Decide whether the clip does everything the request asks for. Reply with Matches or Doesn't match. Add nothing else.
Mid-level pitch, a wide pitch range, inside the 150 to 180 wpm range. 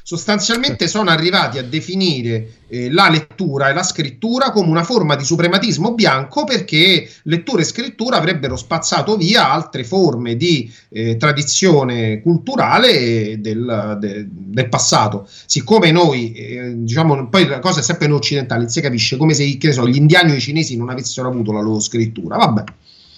Matches